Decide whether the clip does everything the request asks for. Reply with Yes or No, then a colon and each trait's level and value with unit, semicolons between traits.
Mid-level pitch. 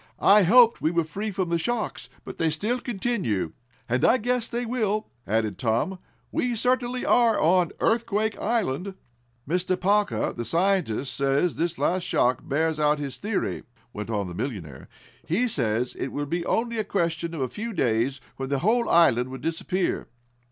Yes: medium, 175 Hz